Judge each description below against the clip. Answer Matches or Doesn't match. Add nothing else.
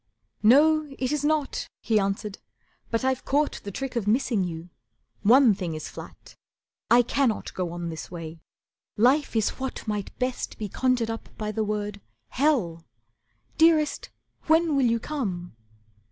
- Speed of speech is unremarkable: Matches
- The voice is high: Matches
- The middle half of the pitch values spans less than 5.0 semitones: Doesn't match